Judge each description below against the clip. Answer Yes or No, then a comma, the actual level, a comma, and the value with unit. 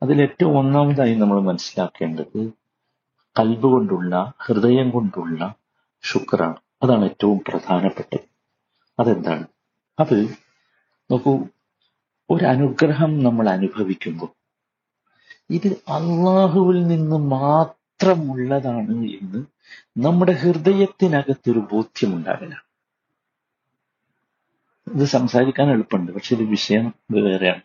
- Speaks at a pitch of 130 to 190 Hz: Yes, low, 135 Hz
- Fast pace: No, average, 80 wpm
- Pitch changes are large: Yes, wide, 6.3 semitones